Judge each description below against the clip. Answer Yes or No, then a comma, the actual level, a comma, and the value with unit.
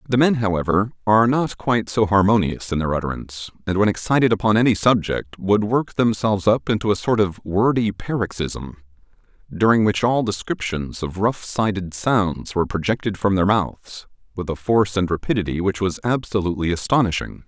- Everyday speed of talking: Yes, average, 170 wpm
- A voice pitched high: No, low, 100 Hz